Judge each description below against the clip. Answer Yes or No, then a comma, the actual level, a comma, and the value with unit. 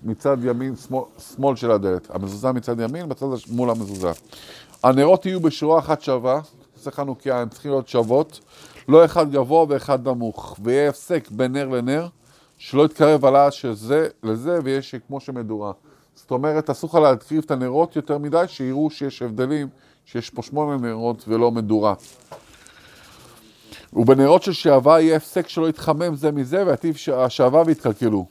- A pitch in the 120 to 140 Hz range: Yes, low, 135 Hz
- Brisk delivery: Yes, fast, 155 wpm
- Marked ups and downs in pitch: No, average, 4.3 semitones